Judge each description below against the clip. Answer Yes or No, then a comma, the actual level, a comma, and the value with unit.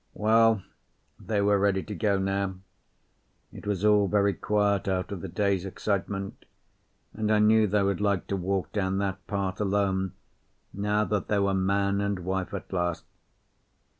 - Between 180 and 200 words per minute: No, average, 160 wpm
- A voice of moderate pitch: No, low, 100 Hz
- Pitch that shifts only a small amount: Yes, narrow, 1.3 semitones